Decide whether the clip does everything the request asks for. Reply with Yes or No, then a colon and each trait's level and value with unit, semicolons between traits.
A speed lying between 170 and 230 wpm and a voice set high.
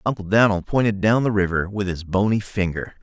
No: average, 200 wpm; low, 100 Hz